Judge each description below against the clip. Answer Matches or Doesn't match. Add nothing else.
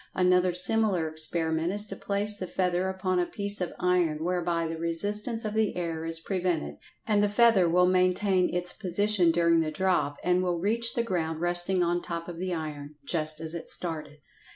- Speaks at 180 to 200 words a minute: Matches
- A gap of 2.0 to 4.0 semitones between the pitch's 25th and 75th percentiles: Matches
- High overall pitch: Doesn't match